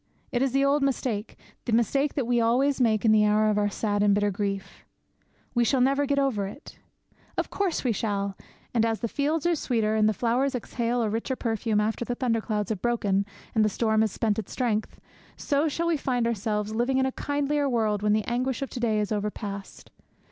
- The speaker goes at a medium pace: No, fast, 220 wpm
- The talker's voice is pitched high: Yes, high, 230 Hz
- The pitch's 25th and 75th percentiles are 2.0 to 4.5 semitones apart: Yes, average, 3.8 semitones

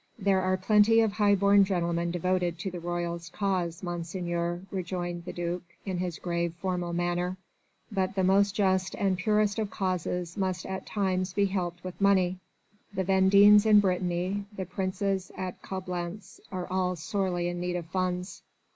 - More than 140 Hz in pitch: Yes, medium, 185 Hz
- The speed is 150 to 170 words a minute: Yes, average, 165 wpm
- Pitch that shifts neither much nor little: No, narrow, 1.9 semitones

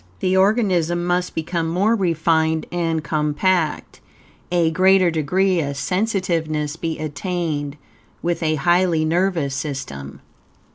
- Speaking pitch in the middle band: Yes, medium, 165 Hz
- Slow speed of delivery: Yes, slow, 110 wpm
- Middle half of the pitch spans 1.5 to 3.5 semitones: Yes, average, 2.8 semitones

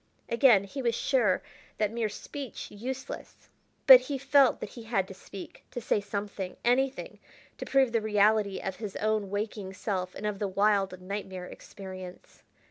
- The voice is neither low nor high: No, high, 210 Hz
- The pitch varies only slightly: No, average, 3.7 semitones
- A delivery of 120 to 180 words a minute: Yes, average, 165 wpm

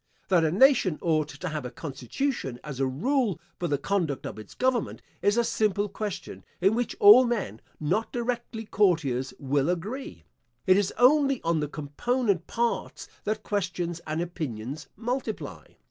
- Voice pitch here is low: No, medium, 185 Hz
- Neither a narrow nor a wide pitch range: No, wide, 7.4 semitones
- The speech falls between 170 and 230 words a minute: No, average, 160 wpm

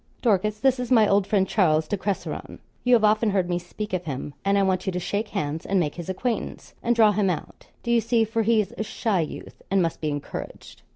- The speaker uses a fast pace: Yes, fast, 240 wpm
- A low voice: No, high, 200 Hz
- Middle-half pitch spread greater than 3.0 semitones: Yes, average, 3.6 semitones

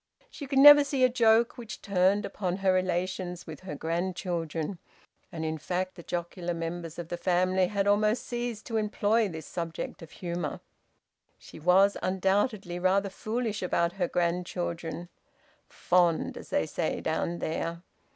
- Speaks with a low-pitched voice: No, medium, 185 Hz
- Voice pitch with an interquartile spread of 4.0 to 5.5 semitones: No, average, 3.2 semitones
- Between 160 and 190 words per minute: No, average, 150 wpm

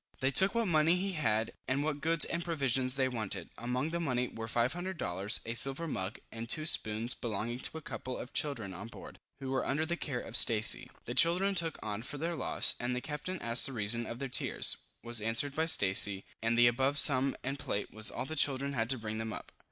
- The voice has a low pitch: Yes, low, 130 Hz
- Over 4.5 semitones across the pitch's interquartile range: Yes, average, 5.2 semitones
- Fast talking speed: Yes, fast, 230 wpm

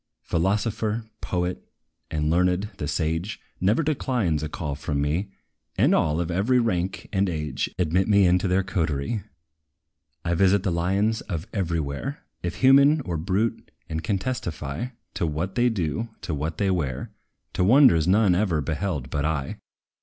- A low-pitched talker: Yes, very low, 90 Hz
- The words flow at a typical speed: Yes, average, 160 wpm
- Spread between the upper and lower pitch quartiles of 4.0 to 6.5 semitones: Yes, average, 4.7 semitones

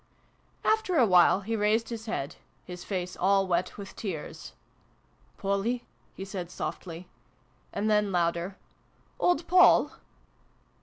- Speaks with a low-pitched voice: No, high, 195 Hz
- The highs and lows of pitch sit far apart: No, average, 3.8 semitones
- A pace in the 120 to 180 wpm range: Yes, average, 140 wpm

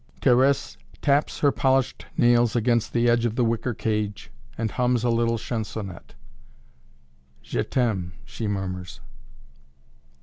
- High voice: No, low, 115 Hz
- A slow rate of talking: Yes, slow, 125 wpm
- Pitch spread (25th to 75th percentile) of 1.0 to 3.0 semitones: Yes, average, 2.7 semitones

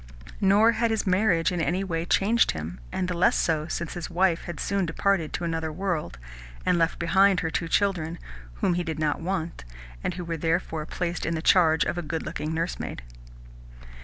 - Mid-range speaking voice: Yes, medium, 170 Hz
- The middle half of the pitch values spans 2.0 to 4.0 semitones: Yes, narrow, 2.6 semitones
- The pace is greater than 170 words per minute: Yes, average, 195 wpm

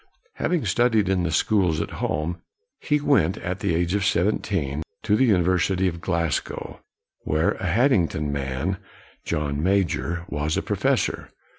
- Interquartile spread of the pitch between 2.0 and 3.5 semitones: No, average, 4.2 semitones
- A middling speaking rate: Yes, average, 150 wpm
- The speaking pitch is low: Yes, very low, 90 Hz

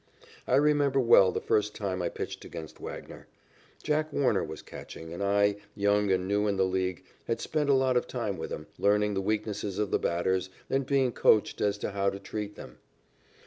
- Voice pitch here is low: Yes, low, 105 Hz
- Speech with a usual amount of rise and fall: Yes, average, 4.2 semitones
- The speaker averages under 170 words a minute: No, average, 200 wpm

